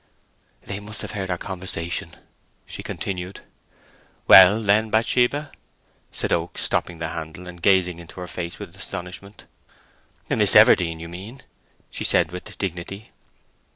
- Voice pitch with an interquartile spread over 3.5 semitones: No, average, 2.8 semitones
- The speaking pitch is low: Yes, very low, 90 Hz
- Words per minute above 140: No, slow, 135 wpm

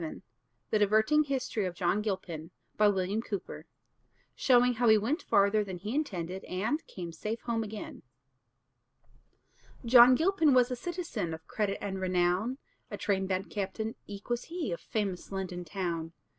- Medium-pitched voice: No, high, 210 Hz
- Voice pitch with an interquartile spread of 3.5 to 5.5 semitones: Yes, average, 4.8 semitones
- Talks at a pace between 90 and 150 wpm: Yes, average, 145 wpm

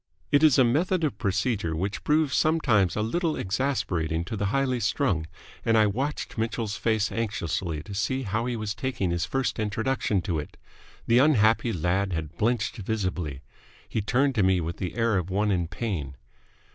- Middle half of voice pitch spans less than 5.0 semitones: No, average, 5.3 semitones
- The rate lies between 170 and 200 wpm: Yes, average, 180 wpm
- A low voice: Yes, low, 105 Hz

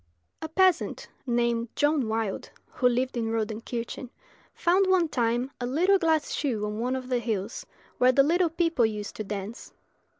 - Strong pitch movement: Yes, wide, 5.7 semitones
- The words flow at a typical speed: Yes, average, 165 wpm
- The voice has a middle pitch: No, high, 245 Hz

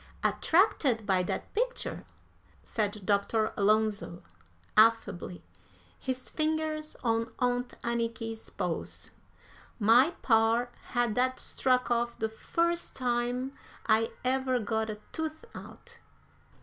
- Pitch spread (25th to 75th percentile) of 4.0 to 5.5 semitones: No, average, 2.8 semitones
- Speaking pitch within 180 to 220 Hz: No, high, 235 Hz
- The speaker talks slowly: Yes, slow, 105 wpm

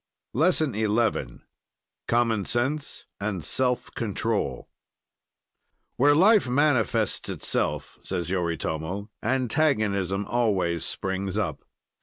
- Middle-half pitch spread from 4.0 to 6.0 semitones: Yes, average, 5.1 semitones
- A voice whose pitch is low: Yes, low, 110 Hz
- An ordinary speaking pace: No, slow, 85 wpm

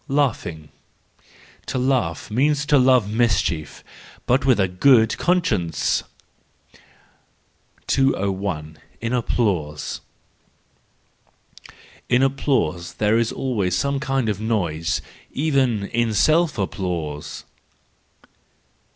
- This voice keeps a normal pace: No, slow, 90 wpm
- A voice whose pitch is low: Yes, low, 115 Hz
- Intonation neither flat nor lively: No, wide, 6.8 semitones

